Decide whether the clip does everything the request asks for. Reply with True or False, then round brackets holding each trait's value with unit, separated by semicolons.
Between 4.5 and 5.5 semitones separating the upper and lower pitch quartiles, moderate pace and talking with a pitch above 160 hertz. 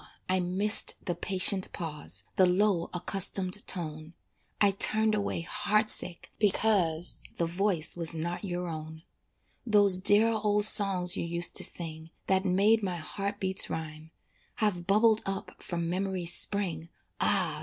False (3.2 semitones; 145 wpm; 185 Hz)